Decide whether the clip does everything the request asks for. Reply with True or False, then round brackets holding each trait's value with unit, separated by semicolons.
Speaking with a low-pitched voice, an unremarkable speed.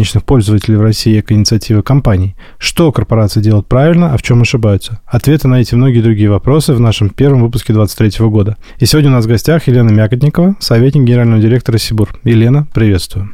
False (115 Hz; 180 wpm)